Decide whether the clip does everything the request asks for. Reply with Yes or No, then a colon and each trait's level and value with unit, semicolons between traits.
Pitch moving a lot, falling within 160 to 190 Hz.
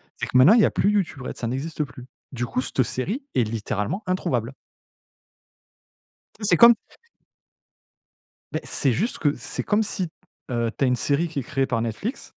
No: wide, 7.3 semitones; low, 135 Hz